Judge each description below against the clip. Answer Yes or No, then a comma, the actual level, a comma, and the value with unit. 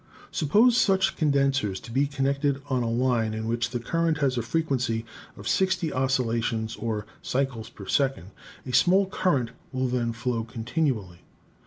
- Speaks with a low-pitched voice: Yes, low, 130 Hz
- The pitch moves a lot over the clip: No, average, 3.7 semitones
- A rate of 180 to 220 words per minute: No, average, 160 wpm